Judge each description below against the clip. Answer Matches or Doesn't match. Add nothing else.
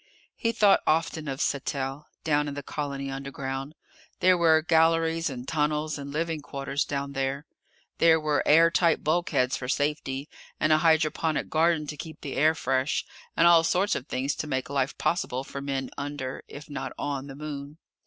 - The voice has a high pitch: Doesn't match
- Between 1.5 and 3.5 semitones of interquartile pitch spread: Matches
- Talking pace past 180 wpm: Doesn't match